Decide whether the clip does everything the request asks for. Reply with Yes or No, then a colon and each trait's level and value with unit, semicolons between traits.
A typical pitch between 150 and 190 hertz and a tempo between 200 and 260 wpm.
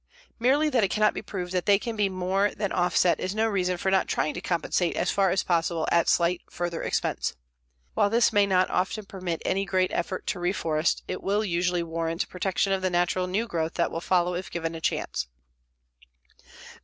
Yes: medium, 185 Hz; fast, 205 wpm